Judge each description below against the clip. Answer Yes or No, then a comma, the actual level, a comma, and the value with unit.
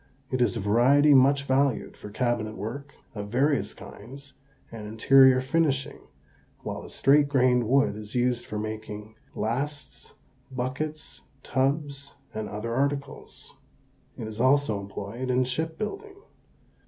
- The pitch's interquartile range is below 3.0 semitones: No, average, 4.2 semitones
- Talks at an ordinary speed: No, slow, 130 wpm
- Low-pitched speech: Yes, low, 130 Hz